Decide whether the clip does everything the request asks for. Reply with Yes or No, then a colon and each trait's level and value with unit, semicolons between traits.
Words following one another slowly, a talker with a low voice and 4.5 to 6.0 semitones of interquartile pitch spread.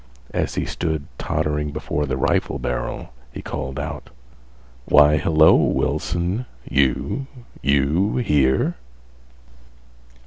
No: slow, 95 wpm; very low, 75 Hz; average, 3.5 semitones